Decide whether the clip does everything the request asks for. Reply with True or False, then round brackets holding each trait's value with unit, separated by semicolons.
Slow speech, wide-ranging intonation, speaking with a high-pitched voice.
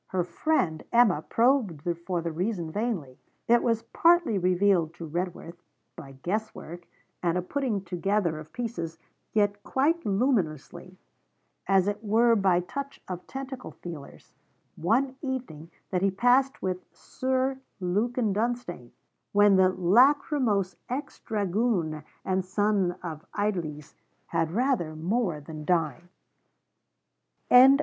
True (125 wpm; 5.7 semitones; 195 Hz)